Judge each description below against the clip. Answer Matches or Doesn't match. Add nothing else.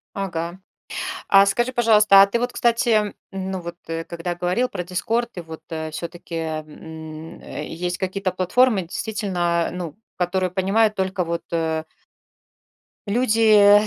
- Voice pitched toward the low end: Doesn't match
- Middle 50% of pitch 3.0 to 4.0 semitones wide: Matches